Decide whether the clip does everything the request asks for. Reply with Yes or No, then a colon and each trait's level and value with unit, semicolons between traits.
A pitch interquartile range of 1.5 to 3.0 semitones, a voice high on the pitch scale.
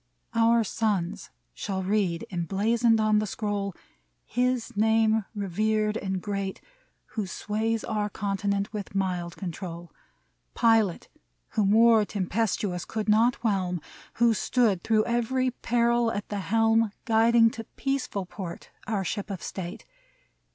Yes: average, 2.7 semitones; high, 210 Hz